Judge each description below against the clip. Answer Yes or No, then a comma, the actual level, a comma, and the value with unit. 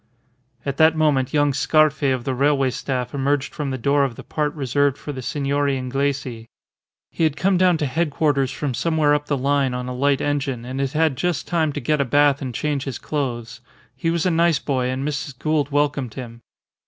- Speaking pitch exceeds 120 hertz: Yes, medium, 140 Hz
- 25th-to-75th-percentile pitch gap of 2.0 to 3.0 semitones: Yes, narrow, 2.4 semitones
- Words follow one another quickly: Yes, fast, 210 wpm